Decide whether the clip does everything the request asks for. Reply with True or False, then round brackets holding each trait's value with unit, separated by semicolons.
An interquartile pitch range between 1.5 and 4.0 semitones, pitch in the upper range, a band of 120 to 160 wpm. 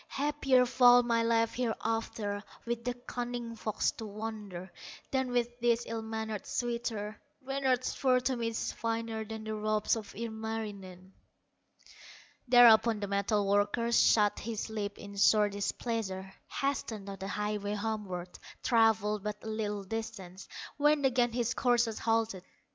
True (2.5 semitones; 225 Hz; 140 wpm)